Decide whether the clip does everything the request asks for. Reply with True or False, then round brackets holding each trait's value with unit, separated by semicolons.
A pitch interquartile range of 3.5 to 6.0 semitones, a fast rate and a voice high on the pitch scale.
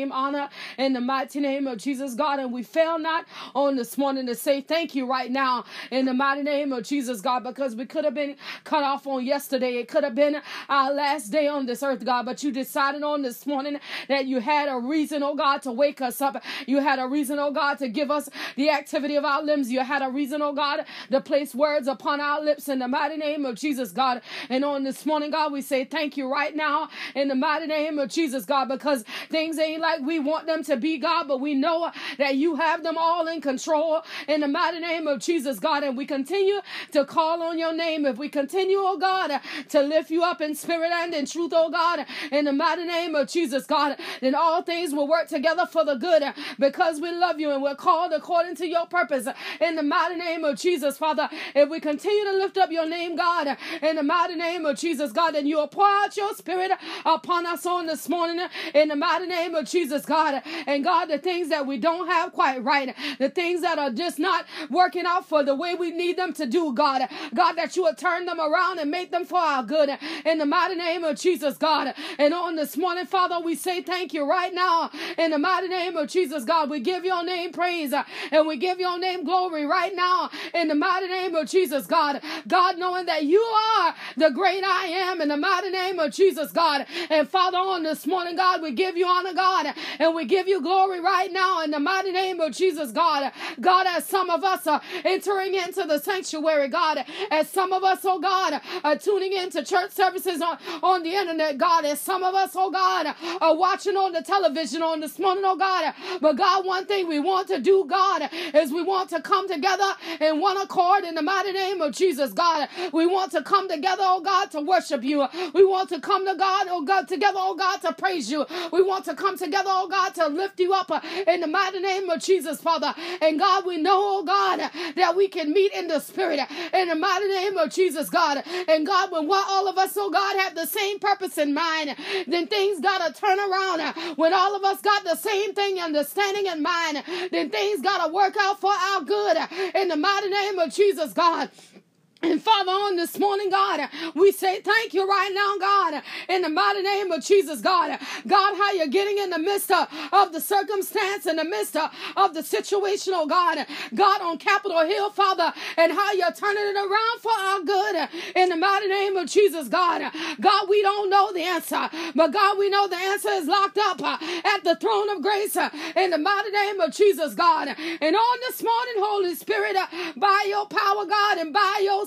True (4.0 semitones; 220 wpm; 335 Hz)